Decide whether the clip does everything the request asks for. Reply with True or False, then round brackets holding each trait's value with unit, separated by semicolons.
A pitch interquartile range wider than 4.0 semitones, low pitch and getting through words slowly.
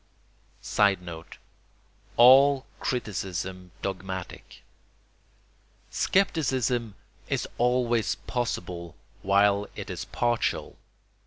True (4.8 semitones; 105 Hz; 65 wpm)